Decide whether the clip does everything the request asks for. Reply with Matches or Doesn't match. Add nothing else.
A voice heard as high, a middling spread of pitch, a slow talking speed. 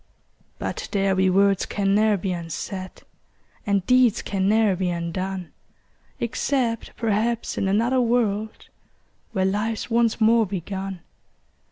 Matches